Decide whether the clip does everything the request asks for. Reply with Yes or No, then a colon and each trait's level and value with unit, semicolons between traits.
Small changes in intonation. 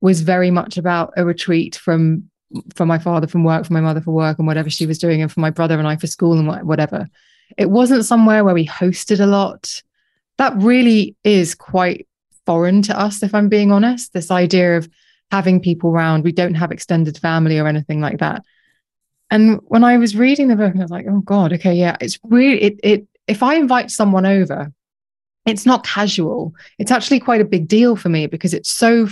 No: average, 4.3 semitones